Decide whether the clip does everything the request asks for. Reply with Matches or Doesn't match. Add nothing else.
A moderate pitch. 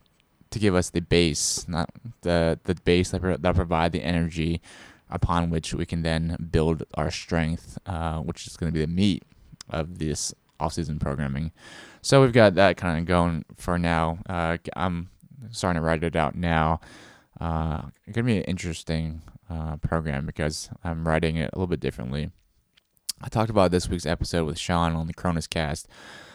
Doesn't match